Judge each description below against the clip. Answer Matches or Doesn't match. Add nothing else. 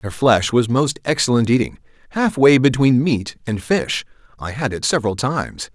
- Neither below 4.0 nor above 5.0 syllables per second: Matches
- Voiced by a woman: Doesn't match